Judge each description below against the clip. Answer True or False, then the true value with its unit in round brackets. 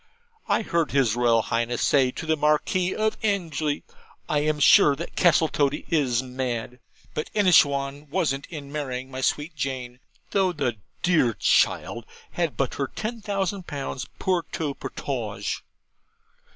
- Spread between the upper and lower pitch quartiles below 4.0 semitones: False (4.5 semitones)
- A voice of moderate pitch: True (145 Hz)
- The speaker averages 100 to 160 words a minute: True (140 wpm)